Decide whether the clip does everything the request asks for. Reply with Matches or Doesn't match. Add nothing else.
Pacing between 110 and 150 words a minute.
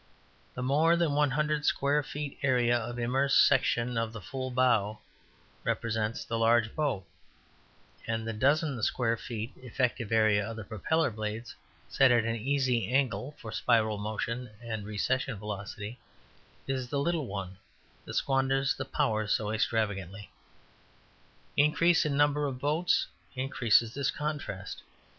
Matches